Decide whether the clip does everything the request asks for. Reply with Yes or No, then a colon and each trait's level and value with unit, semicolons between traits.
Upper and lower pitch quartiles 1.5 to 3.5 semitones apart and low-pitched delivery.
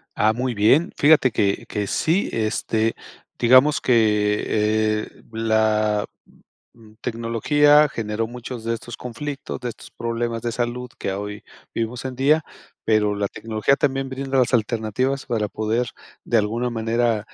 Yes: average, 2.8 semitones; low, 115 Hz